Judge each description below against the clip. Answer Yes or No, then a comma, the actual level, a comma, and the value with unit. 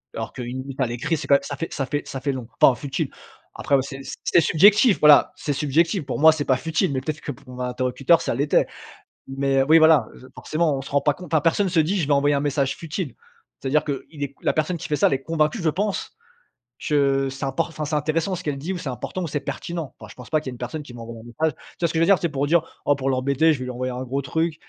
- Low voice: No, medium, 145 Hz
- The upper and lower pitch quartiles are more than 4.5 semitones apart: No, average, 3.1 semitones